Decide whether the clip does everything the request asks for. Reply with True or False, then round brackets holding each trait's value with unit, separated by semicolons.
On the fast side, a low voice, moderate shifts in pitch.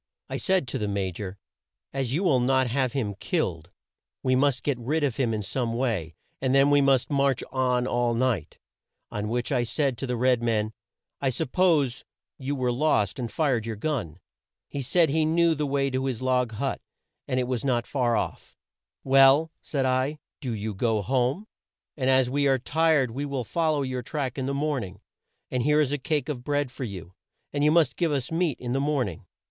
True (210 wpm; 130 Hz; 3.2 semitones)